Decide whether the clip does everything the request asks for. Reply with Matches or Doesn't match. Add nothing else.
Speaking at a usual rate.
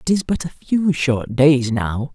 Doesn't match